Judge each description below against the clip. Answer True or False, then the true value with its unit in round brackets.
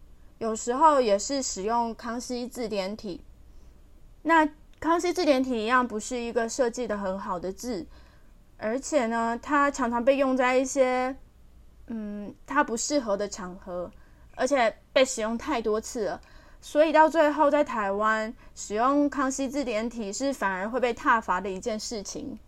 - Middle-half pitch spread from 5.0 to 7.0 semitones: False (4.5 semitones)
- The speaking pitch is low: False (235 Hz)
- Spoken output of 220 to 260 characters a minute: True (230 characters per minute)